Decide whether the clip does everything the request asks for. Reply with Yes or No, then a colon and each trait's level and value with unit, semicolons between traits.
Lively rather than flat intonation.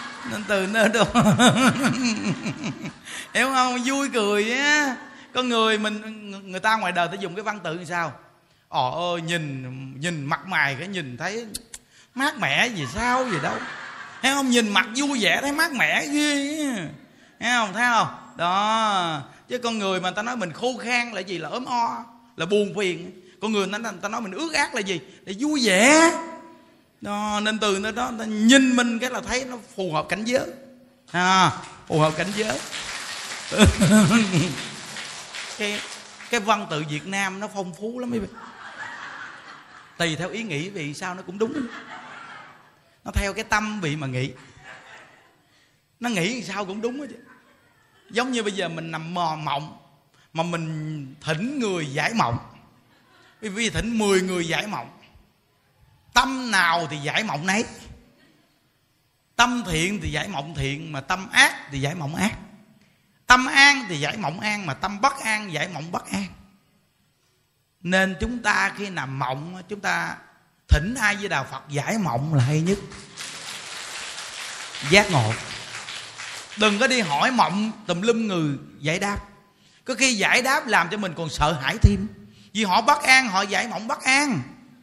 Yes: wide, 5.8 semitones